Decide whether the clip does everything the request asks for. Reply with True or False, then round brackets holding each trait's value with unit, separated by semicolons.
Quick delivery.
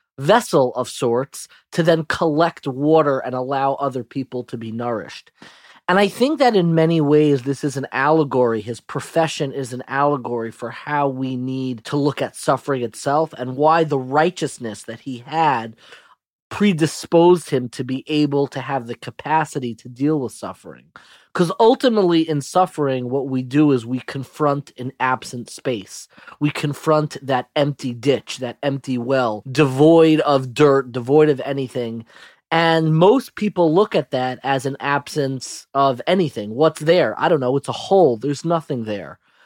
False (165 wpm)